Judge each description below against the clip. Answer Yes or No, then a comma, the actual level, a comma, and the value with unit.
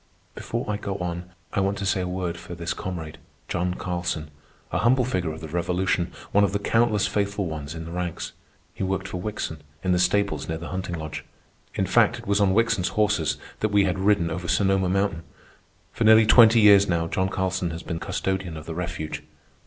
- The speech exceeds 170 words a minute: Yes, fast, 205 wpm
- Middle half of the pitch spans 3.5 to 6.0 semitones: No, average, 2.9 semitones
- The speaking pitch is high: No, very low, 95 Hz